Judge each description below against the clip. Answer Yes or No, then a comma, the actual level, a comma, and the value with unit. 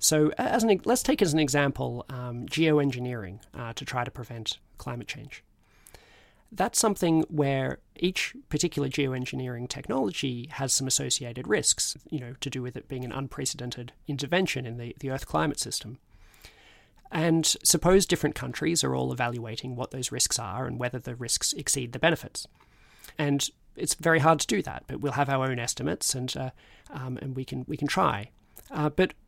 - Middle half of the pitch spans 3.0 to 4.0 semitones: Yes, average, 3.6 semitones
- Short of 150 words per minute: No, average, 175 wpm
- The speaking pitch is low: Yes, low, 130 Hz